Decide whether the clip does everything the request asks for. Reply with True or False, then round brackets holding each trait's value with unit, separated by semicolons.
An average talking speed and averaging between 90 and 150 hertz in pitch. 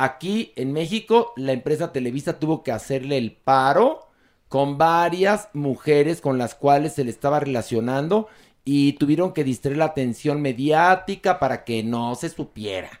True (150 wpm; 140 Hz)